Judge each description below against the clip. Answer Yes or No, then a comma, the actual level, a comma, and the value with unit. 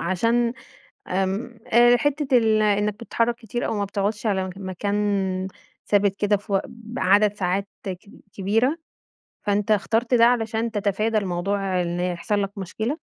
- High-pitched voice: Yes, high, 205 Hz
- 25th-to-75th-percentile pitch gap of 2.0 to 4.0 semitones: Yes, average, 2.9 semitones